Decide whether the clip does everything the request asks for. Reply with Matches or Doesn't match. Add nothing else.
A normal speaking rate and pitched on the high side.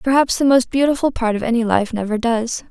Doesn't match